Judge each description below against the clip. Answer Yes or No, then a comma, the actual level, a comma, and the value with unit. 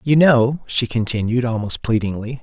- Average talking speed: Yes, average, 150 wpm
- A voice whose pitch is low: Yes, low, 120 Hz